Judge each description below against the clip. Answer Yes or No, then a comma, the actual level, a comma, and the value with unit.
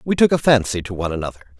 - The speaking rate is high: Yes, fast, 265 wpm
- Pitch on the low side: Yes, low, 110 Hz